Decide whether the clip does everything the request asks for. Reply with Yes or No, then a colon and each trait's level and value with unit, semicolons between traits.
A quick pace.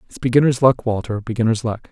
No: average, 190 wpm